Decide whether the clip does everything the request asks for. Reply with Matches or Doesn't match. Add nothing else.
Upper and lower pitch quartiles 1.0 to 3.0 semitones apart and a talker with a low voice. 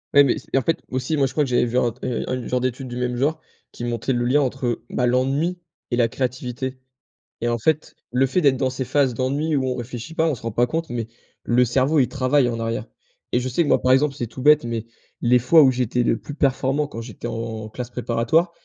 Matches